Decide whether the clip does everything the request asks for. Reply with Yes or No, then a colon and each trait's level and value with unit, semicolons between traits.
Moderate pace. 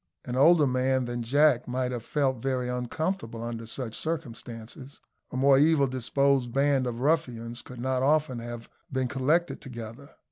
Yes: average, 155 wpm